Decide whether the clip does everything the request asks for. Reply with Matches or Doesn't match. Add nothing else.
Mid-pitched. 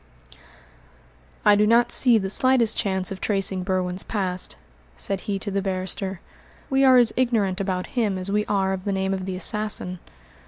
Doesn't match